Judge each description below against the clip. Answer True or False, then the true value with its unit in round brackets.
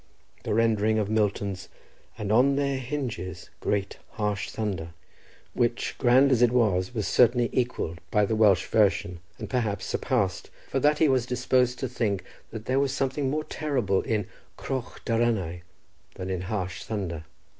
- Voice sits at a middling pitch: False (110 Hz)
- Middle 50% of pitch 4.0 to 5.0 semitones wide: True (4.4 semitones)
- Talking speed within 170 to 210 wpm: False (155 wpm)